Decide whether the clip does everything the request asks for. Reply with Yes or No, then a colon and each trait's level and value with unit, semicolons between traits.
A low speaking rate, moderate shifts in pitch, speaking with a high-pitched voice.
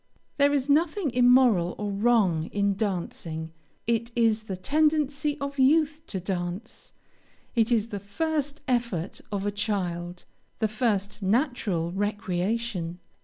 No: slow, 125 wpm; wide, 5.7 semitones; high, 215 Hz